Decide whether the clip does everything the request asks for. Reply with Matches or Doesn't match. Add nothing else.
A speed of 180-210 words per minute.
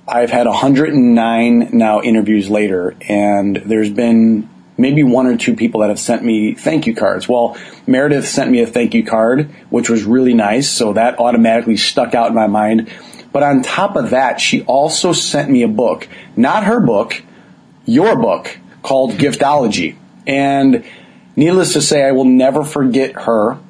Doesn't match